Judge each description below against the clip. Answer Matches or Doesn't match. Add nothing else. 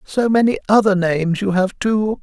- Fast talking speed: Doesn't match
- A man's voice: Matches